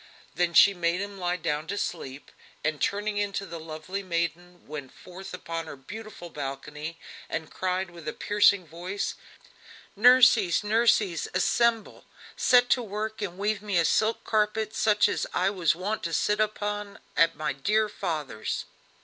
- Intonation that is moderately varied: Yes, average, 4.0 semitones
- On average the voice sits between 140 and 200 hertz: Yes, medium, 185 Hz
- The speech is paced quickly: No, average, 160 wpm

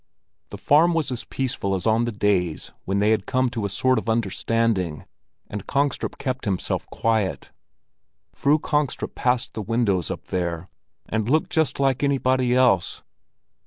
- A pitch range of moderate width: Yes, average, 4.7 semitones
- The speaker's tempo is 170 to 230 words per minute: No, average, 160 wpm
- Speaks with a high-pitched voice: No, low, 115 Hz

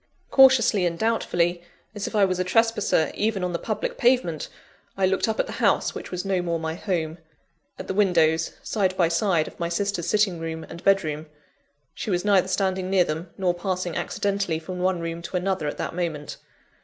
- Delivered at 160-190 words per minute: No, fast, 205 wpm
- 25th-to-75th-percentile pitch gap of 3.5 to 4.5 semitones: No, average, 2.8 semitones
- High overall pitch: No, medium, 180 Hz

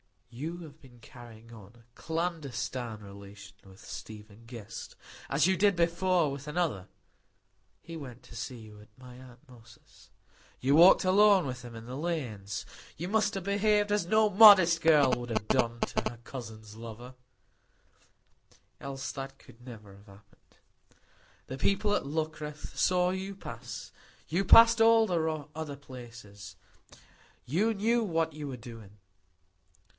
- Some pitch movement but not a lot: No, wide, 7.1 semitones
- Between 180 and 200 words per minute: No, average, 145 wpm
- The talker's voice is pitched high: No, low, 135 Hz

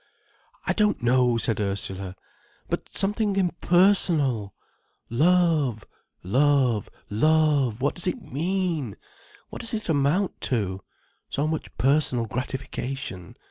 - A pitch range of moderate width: No, wide, 6.9 semitones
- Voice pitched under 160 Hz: Yes, medium, 140 Hz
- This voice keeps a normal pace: No, slow, 90 wpm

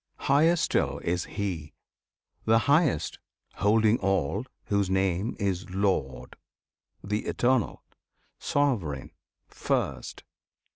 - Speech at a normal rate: No, slow, 90 wpm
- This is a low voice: Yes, low, 100 Hz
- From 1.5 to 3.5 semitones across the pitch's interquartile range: No, average, 4.5 semitones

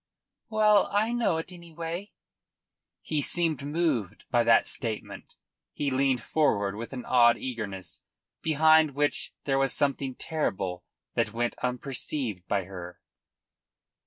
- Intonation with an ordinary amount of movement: No, wide, 5.8 semitones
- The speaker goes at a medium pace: No, slow, 125 wpm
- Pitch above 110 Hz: Yes, low, 135 Hz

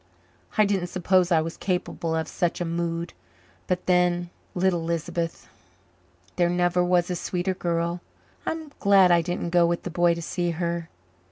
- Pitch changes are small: Yes, narrow, 1.1 semitones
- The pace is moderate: Yes, average, 165 wpm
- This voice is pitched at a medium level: Yes, medium, 175 Hz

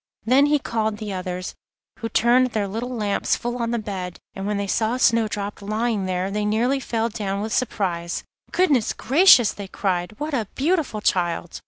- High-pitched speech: Yes, high, 215 Hz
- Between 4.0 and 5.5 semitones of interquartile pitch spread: No, average, 3.4 semitones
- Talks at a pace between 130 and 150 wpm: No, average, 180 wpm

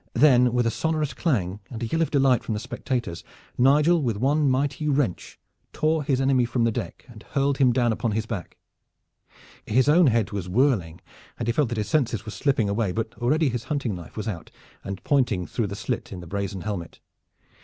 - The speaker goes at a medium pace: No, fast, 210 wpm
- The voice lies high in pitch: No, low, 120 Hz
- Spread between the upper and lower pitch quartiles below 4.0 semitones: No, average, 4.7 semitones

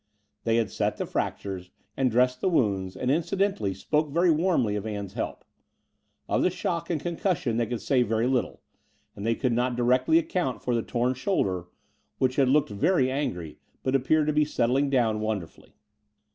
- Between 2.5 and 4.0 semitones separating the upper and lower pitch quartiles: No, wide, 5.5 semitones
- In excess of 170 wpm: Yes, average, 185 wpm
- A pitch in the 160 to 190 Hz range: No, low, 125 Hz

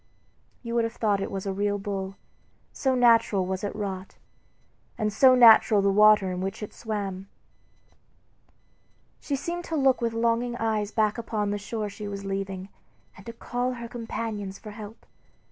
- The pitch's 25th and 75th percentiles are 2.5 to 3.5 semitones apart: Yes, average, 2.9 semitones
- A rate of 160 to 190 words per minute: Yes, average, 175 wpm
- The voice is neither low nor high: No, high, 210 Hz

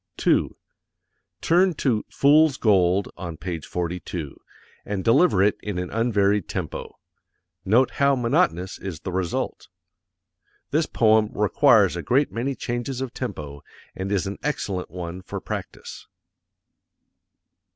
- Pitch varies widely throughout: Yes, wide, 5.7 semitones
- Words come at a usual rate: No, slow, 130 wpm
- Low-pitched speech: Yes, low, 100 Hz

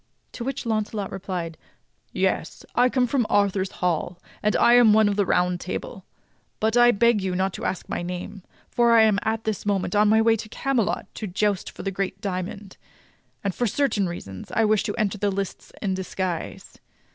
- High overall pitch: Yes, high, 205 Hz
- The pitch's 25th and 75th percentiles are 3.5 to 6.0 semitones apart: No, average, 2.9 semitones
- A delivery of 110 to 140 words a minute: No, average, 190 wpm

